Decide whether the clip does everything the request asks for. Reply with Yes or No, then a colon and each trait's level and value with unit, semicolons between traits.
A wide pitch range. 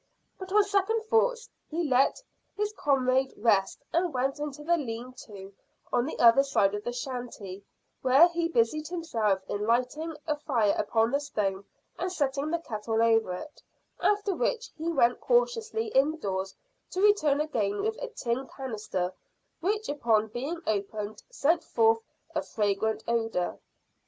Yes: wide, 7.2 semitones